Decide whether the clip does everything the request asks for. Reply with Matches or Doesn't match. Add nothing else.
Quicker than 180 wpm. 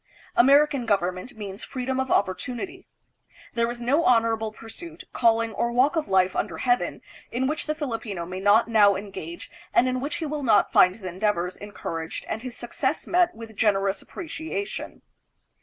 Doesn't match